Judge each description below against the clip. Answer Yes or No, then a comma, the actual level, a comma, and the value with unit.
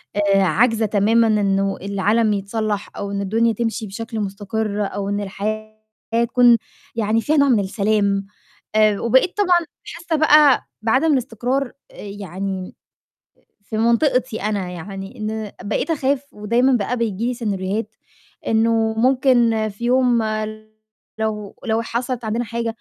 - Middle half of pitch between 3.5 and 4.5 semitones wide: No, average, 2.9 semitones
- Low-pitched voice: No, high, 220 Hz